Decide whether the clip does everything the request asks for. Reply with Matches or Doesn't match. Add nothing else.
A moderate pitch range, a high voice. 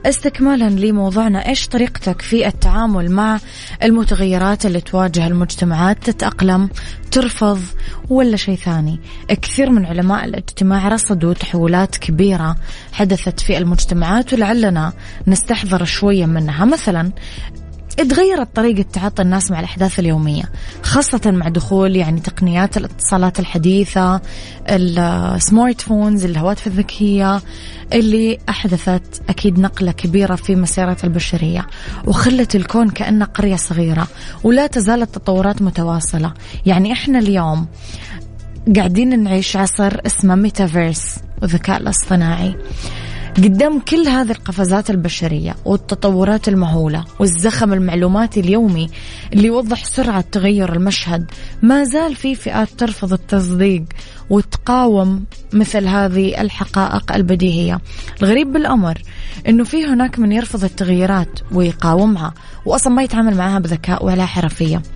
Matches